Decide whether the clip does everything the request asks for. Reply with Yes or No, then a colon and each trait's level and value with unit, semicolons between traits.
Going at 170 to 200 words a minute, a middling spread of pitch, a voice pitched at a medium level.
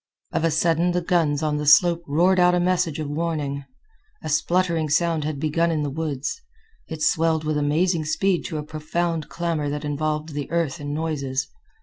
No: average, 190 wpm; narrow, 2.3 semitones; medium, 155 Hz